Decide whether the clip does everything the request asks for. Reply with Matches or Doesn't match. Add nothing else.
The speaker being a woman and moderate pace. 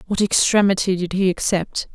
Matches